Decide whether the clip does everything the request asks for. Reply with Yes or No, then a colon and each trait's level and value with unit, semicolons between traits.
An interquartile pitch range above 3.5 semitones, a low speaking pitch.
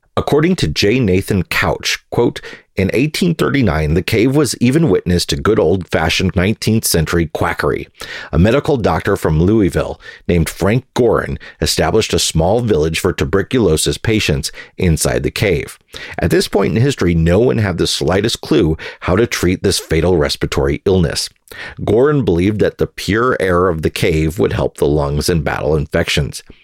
Yes: average, 4.2 semitones; very low, 85 Hz